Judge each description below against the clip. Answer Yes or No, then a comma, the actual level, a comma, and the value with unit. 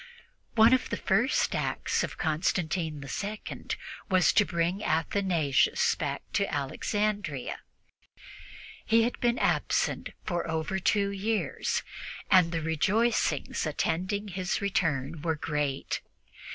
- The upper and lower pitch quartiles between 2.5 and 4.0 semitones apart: No, average, 4.6 semitones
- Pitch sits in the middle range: Yes, medium, 180 Hz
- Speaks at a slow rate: Yes, slow, 110 wpm